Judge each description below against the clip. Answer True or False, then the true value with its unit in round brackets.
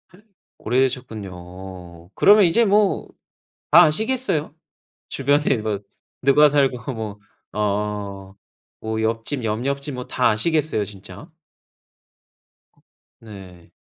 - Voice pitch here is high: False (115 Hz)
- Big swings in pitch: True (6.3 semitones)